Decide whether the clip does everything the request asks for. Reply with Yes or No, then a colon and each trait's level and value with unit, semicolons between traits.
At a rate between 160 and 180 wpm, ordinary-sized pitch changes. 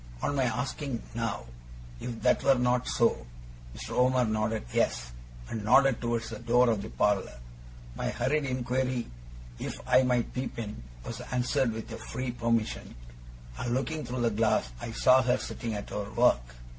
No: average, 170 wpm; narrow, 2.3 semitones